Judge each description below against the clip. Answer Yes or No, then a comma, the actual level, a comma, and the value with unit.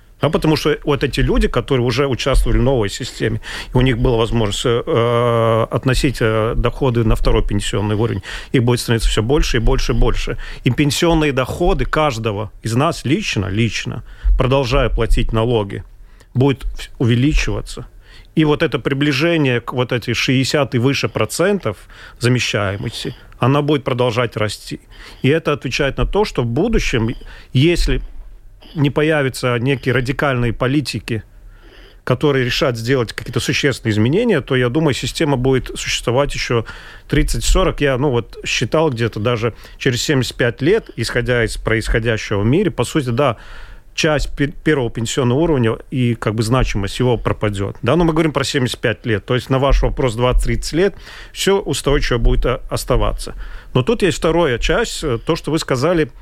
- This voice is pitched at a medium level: No, low, 125 Hz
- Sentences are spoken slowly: No, average, 155 wpm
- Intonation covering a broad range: No, average, 3.8 semitones